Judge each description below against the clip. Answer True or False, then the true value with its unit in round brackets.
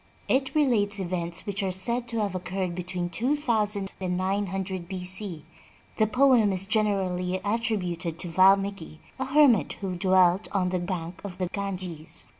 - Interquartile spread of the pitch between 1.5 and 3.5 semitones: True (2.7 semitones)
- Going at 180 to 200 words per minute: False (170 wpm)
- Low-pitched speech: False (190 Hz)